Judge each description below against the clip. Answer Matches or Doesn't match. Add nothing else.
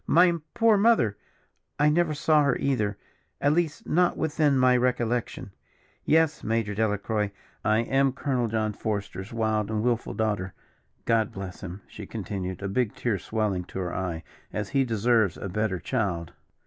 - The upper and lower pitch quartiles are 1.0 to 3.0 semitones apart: Doesn't match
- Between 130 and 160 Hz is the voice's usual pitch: Doesn't match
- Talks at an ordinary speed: Matches